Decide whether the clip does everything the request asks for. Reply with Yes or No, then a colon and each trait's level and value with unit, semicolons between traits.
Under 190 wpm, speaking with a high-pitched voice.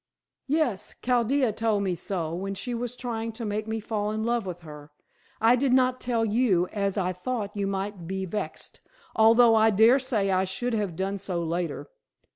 No: average, 195 wpm; high, 210 Hz